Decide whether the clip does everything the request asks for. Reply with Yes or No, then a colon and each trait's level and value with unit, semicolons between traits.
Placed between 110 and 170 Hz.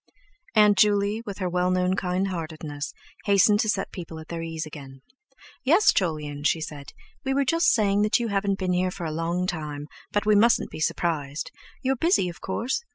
No: medium, 185 Hz